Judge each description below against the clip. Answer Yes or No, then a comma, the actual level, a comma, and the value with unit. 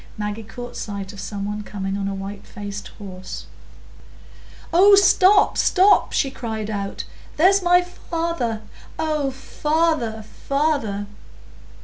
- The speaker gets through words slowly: Yes, slow, 120 wpm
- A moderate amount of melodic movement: No, wide, 8.3 semitones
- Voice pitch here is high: Yes, high, 225 Hz